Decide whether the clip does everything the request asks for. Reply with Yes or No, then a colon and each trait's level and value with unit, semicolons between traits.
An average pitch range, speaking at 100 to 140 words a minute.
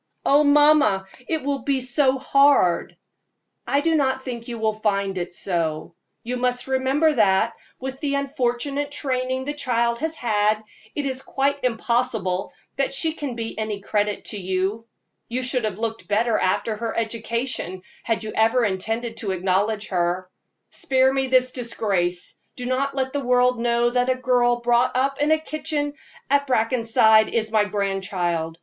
No: average, 3.9 semitones; average, 165 wpm